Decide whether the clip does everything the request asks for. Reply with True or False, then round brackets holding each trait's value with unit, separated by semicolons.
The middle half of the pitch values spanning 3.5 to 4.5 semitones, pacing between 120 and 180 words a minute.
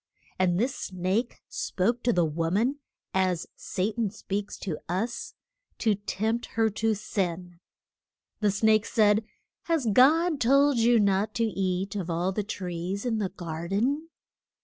True (4.1 semitones; 150 wpm)